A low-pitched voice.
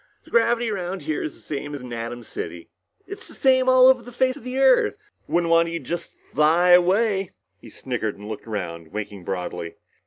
No: medium, 170 Hz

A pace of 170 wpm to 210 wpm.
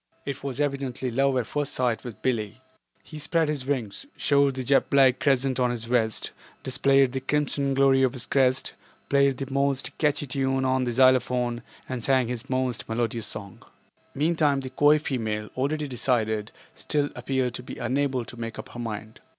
Yes: average, 180 wpm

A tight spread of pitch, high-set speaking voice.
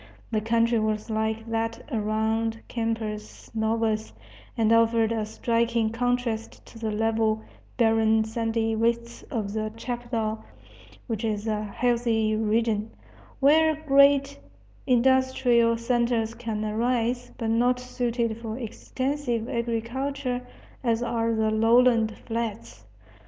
Yes: narrow, 1.6 semitones; high, 230 Hz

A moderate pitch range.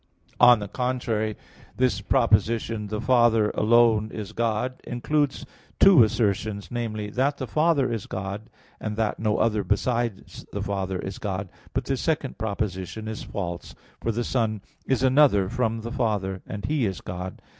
Yes: average, 3.1 semitones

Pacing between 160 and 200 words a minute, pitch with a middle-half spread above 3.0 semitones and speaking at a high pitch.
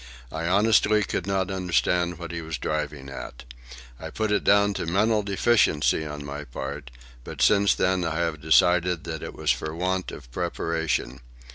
No: average, 170 wpm; average, 4.0 semitones; very low, 85 Hz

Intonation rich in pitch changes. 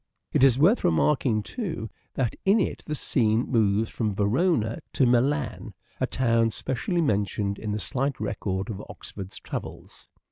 No: average, 4.8 semitones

